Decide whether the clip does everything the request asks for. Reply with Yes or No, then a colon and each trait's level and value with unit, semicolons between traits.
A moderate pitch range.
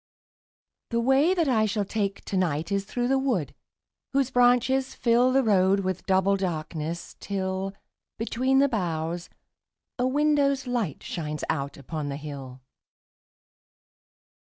No: wide, 7.0 semitones